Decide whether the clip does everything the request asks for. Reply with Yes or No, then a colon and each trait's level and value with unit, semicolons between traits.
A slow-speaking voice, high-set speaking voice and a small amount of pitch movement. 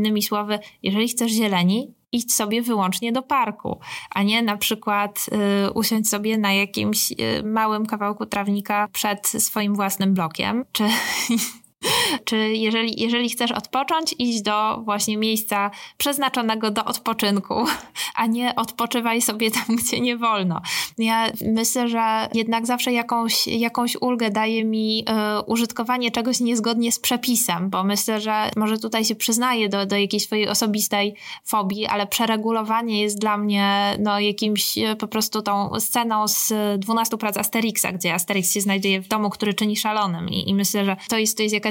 No: fast, 160 wpm; high, 220 Hz; narrow, 2.0 semitones